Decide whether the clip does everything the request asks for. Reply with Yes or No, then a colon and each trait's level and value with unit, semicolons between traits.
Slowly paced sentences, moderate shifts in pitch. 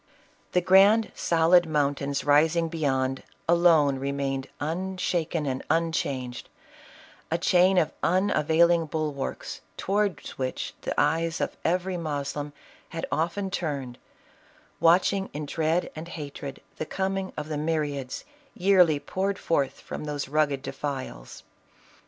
Yes: slow, 120 wpm; average, 3.6 semitones